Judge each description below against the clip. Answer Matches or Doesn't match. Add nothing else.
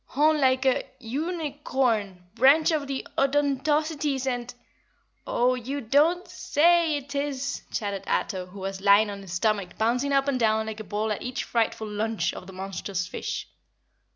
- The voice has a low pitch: Doesn't match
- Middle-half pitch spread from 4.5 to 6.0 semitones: Matches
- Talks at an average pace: Matches